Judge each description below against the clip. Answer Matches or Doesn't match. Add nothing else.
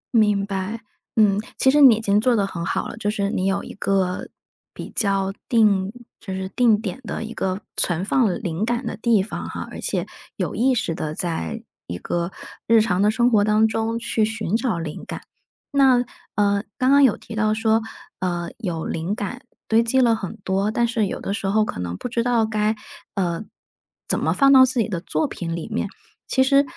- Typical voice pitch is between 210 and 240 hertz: Matches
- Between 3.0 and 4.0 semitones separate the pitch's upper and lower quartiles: Matches